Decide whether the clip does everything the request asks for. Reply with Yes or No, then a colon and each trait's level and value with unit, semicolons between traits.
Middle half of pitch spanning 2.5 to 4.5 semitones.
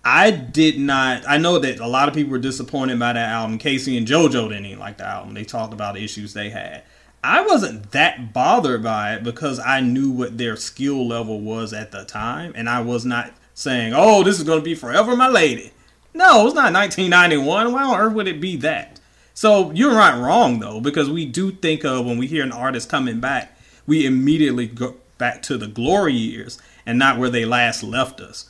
No: average, 5.2 semitones